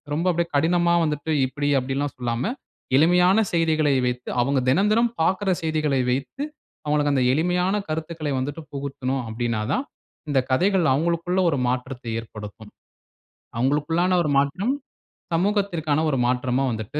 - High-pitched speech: No, medium, 150 Hz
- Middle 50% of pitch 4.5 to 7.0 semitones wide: Yes, average, 4.8 semitones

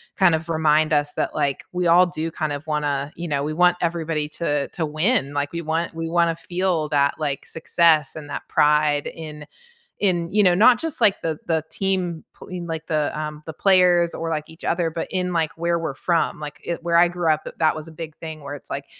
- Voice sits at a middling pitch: Yes, medium, 160 Hz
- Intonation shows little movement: Yes, narrow, 2.3 semitones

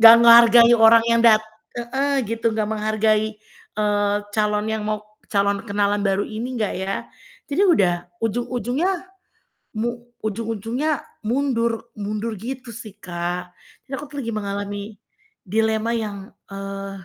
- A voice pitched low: No, high, 220 Hz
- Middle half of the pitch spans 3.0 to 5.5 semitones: No, narrow, 2.4 semitones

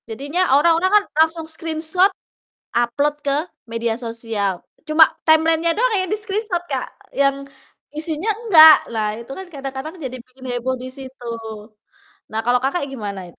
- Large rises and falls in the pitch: No, average, 5.0 semitones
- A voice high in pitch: Yes, very high, 280 Hz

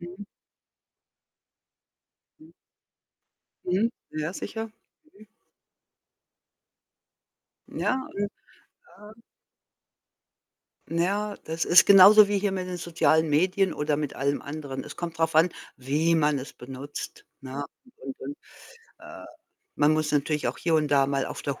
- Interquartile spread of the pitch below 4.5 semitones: No, average, 5.1 semitones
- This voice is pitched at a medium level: Yes, medium, 160 Hz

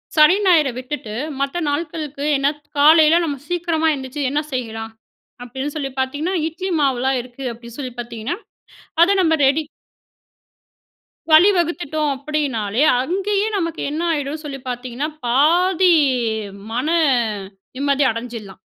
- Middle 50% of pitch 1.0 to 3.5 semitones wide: No, average, 4.1 semitones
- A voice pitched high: Yes, very high, 290 Hz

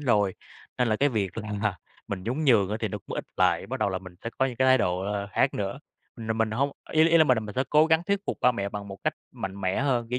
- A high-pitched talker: No, low, 110 Hz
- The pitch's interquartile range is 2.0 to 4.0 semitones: No, average, 4.6 semitones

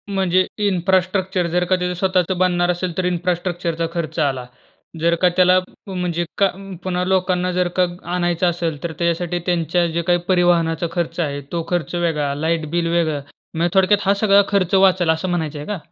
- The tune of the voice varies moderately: No, narrow, 1.7 semitones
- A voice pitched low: No, medium, 175 Hz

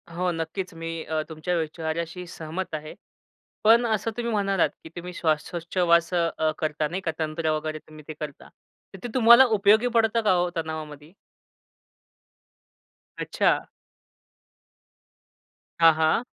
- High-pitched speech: No, medium, 170 Hz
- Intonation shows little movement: No, average, 3.4 semitones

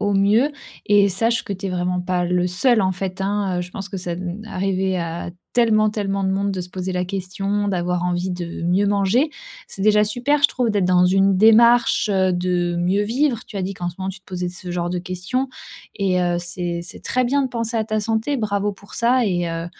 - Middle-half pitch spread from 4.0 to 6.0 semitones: No, average, 3.0 semitones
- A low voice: No, high, 195 Hz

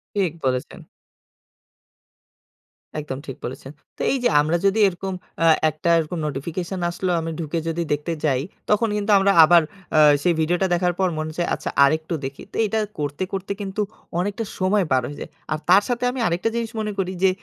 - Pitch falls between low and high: Yes, medium, 175 Hz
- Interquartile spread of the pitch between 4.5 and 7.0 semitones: No, average, 4.0 semitones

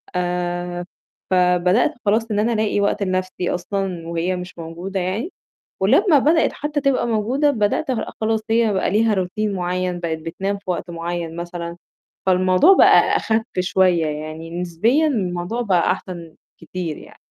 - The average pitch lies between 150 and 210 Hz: Yes, medium, 185 Hz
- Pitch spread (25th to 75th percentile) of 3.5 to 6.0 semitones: Yes, average, 3.9 semitones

